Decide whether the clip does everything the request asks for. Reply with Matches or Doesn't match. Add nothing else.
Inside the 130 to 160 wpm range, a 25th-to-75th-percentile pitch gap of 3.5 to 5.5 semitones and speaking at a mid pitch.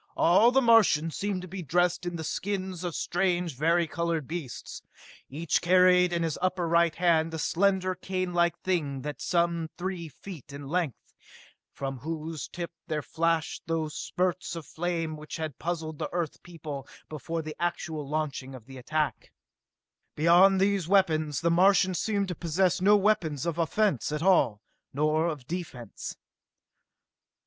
Doesn't match